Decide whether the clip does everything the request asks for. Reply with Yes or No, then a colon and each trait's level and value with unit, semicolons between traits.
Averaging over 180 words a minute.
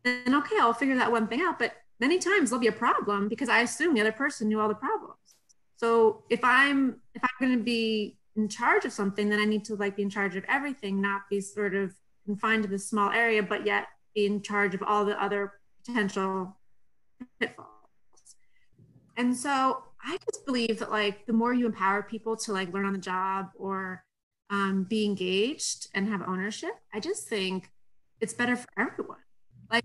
Yes: average, 200 wpm